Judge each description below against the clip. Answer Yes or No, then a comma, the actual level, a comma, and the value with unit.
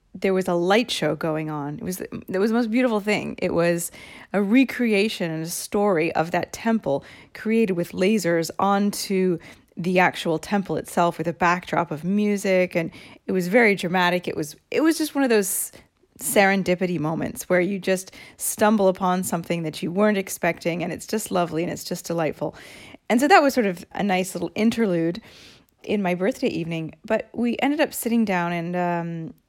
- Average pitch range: Yes, average, 3.7 semitones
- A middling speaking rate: Yes, average, 190 wpm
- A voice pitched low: No, medium, 185 Hz